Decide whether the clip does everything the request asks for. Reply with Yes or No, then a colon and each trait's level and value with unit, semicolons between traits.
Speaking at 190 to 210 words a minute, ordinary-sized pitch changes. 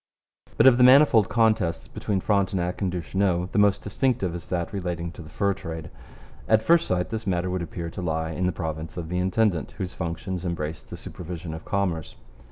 Yes: average, 195 wpm; average, 3.1 semitones